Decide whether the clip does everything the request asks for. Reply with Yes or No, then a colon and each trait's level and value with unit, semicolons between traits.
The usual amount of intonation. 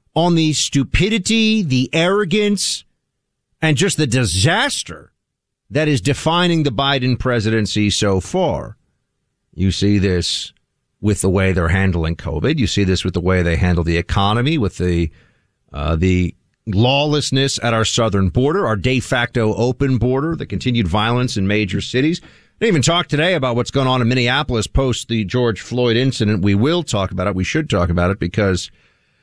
No: wide, 6.4 semitones